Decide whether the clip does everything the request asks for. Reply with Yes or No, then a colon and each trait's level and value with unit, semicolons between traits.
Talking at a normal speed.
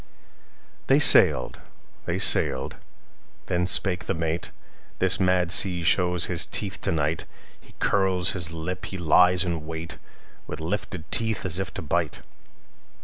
No: slow, 130 wpm